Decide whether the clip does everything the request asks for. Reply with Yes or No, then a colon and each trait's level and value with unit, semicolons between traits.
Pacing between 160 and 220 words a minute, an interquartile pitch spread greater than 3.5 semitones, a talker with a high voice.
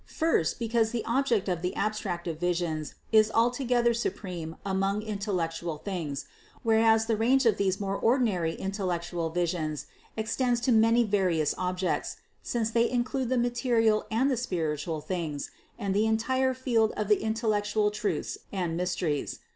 No: average, 150 wpm; average, 4.7 semitones; high, 210 Hz